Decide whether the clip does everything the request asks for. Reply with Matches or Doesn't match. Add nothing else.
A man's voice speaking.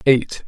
Matches